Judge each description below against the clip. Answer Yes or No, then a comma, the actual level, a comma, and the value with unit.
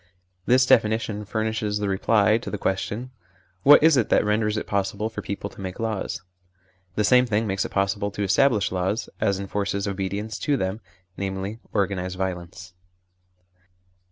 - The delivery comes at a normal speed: Yes, average, 155 wpm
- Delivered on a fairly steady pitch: Yes, narrow, 2.2 semitones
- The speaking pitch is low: Yes, low, 105 Hz